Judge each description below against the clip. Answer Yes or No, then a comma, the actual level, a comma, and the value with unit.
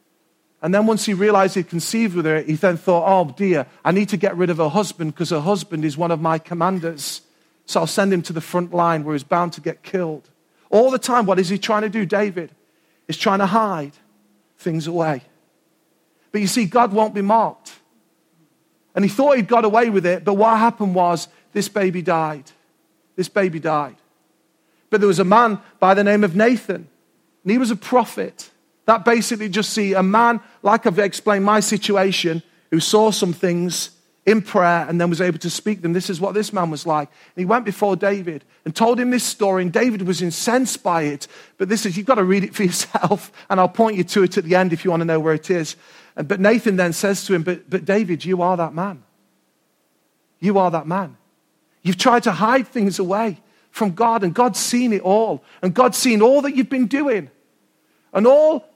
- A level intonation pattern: No, average, 4.2 semitones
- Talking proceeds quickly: Yes, fast, 220 wpm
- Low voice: No, high, 190 Hz